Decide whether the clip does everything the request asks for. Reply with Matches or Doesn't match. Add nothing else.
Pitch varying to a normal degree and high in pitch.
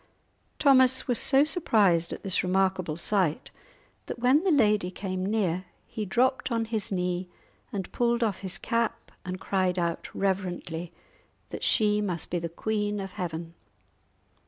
Matches